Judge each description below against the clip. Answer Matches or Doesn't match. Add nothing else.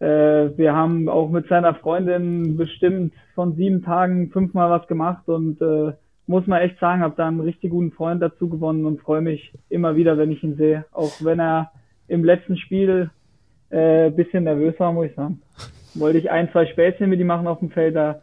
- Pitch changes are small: Matches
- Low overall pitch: Doesn't match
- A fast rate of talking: Matches